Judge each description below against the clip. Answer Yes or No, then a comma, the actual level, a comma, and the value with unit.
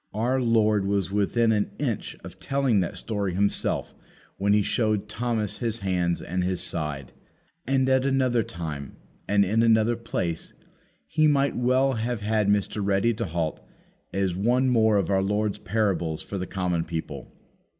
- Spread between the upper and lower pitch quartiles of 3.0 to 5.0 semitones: Yes, average, 3.9 semitones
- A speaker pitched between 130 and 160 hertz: No, low, 105 Hz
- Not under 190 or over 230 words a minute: No, average, 160 wpm